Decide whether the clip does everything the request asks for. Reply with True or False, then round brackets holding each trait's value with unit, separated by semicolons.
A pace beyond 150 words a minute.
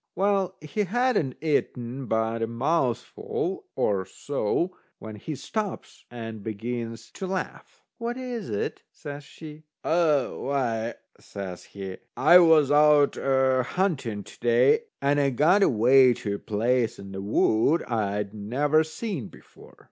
False (140 wpm)